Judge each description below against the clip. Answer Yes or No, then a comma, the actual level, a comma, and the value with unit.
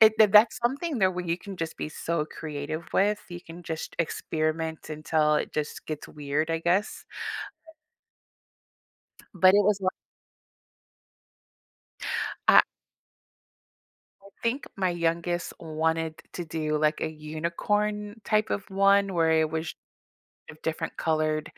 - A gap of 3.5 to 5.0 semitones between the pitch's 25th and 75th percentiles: Yes, average, 4.0 semitones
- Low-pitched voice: No, medium, 165 Hz